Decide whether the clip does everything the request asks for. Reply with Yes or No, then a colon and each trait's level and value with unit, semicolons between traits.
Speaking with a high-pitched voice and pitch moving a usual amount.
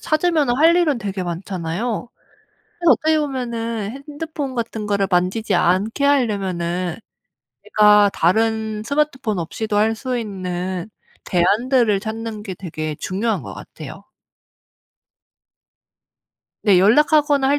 No: high, 220 Hz; wide, 5.7 semitones